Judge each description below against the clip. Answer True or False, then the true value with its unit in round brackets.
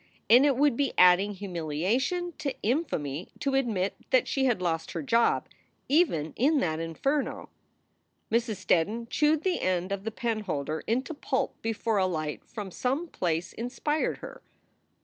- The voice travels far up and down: True (7.2 semitones)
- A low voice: False (225 Hz)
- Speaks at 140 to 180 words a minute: True (155 wpm)